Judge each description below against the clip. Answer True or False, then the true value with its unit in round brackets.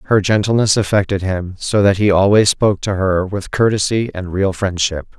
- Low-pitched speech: True (100 Hz)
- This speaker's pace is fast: False (185 wpm)